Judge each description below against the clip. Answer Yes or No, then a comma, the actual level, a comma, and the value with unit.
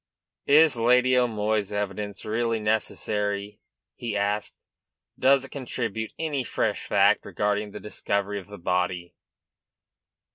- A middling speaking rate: No, slow, 115 wpm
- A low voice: Yes, low, 105 Hz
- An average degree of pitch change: Yes, average, 3.0 semitones